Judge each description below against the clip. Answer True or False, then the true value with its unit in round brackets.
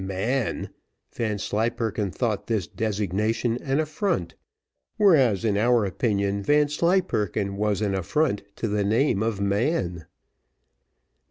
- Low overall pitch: True (110 Hz)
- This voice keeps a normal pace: False (105 wpm)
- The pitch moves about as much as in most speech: True (4.4 semitones)